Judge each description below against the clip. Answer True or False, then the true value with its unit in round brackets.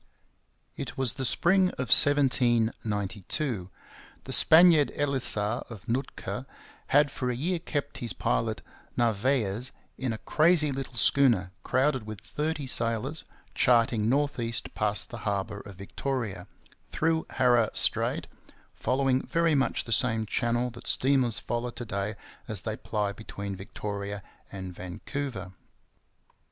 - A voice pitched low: True (120 Hz)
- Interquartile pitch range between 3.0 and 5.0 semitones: True (4.6 semitones)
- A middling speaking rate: False (130 wpm)